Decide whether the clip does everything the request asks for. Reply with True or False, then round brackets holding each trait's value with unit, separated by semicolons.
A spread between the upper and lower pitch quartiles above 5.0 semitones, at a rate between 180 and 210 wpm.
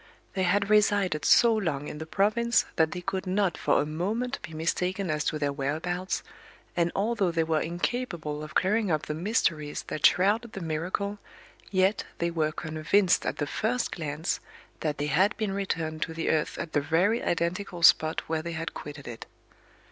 False (4.2 semitones; 185 wpm)